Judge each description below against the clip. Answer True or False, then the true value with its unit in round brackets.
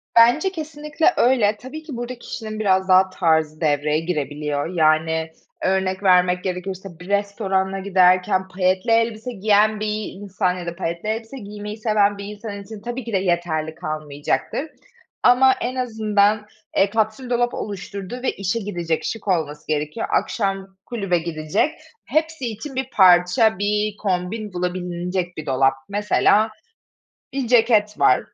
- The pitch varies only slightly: False (3.7 semitones)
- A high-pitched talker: True (200 Hz)